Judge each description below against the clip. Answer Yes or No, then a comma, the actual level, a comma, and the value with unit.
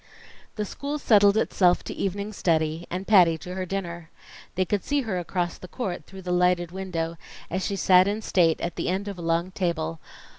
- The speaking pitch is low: No, medium, 180 Hz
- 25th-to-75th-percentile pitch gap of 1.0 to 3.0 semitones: Yes, narrow, 2.5 semitones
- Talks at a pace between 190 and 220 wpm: Yes, average, 200 wpm